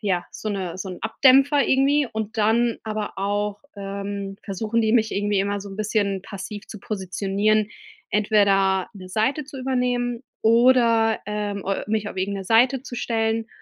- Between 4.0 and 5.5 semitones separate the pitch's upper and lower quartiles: No, narrow, 2.6 semitones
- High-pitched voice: Yes, high, 215 Hz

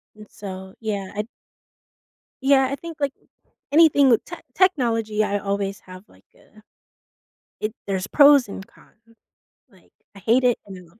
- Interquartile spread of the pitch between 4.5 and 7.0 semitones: Yes, average, 5.2 semitones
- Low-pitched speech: No, high, 215 Hz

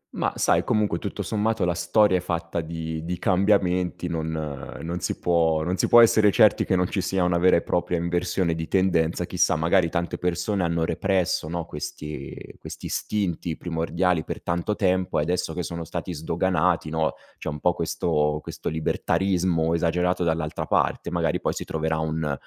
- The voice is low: Yes, very low, 85 Hz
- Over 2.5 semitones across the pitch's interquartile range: No, narrow, 2.0 semitones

